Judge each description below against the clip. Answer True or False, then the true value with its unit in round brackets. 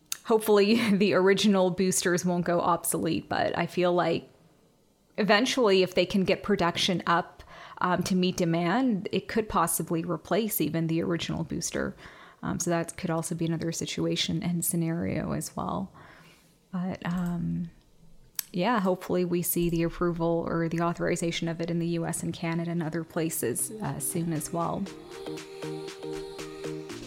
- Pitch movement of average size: False (1.8 semitones)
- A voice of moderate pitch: True (170 Hz)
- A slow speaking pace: False (150 wpm)